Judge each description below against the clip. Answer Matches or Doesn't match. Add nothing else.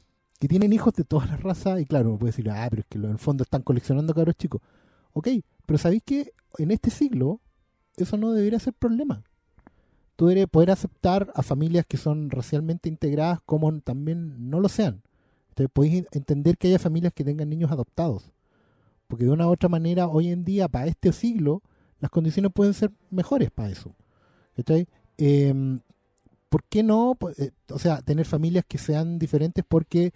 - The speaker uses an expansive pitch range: Doesn't match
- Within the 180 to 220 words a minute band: Matches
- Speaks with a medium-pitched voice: Matches